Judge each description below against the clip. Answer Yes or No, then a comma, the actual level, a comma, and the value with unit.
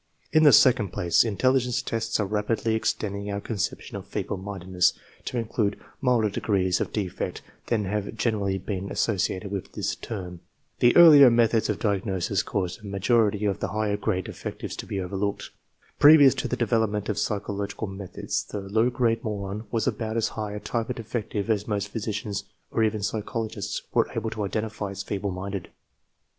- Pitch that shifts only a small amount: Yes, narrow, 2.3 semitones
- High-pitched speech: No, low, 105 Hz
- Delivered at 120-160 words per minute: No, average, 180 wpm